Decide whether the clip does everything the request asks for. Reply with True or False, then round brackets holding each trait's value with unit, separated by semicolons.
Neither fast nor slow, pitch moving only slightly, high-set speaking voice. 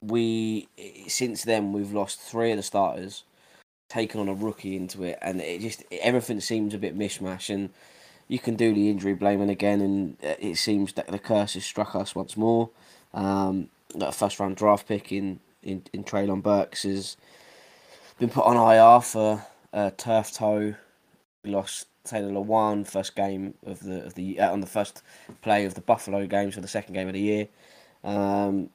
False (190 wpm; 1.8 semitones; 100 Hz)